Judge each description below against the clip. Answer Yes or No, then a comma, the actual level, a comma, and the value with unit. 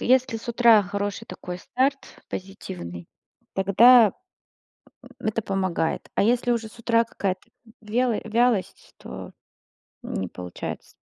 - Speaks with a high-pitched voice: Yes, high, 215 Hz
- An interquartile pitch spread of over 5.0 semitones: No, average, 3.8 semitones